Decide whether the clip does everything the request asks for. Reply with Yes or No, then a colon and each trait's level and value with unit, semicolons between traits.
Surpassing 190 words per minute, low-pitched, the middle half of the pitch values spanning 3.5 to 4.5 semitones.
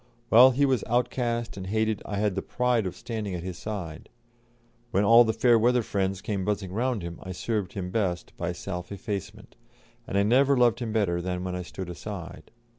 Yes: average, 200 wpm; low, 105 Hz; average, 4.1 semitones